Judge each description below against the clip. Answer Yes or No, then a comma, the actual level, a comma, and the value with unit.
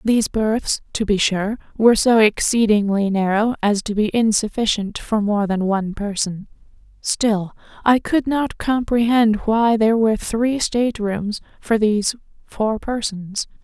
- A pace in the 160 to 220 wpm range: No, average, 145 wpm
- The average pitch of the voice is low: No, high, 215 Hz